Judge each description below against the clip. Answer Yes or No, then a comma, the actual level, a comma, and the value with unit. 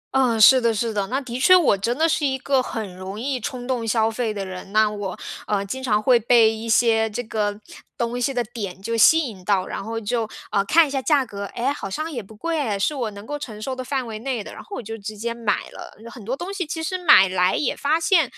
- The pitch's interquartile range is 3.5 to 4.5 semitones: Yes, average, 4.2 semitones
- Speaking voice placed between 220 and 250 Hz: Yes, high, 230 Hz